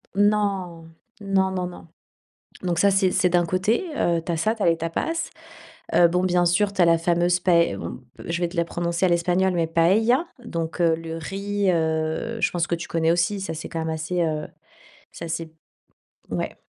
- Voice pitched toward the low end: No, medium, 175 Hz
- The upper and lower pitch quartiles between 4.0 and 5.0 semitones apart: No, narrow, 2.4 semitones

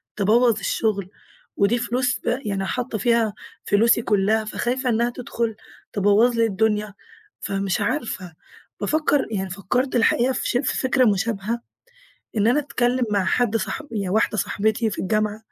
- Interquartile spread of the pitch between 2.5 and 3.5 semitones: Yes, average, 3.1 semitones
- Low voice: No, high, 220 Hz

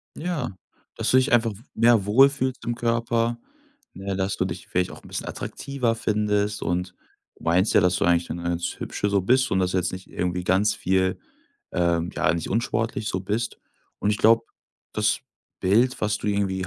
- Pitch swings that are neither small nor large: Yes, average, 4.0 semitones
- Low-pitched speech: Yes, low, 105 Hz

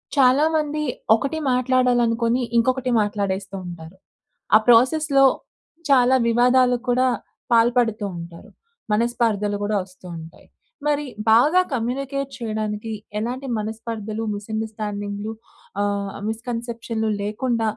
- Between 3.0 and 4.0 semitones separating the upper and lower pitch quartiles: Yes, average, 3.3 semitones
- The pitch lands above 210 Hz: Yes, high, 230 Hz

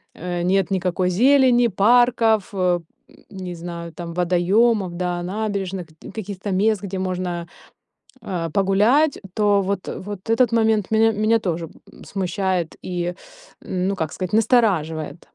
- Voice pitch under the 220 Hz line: Yes, high, 190 Hz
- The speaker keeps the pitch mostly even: No, average, 3.6 semitones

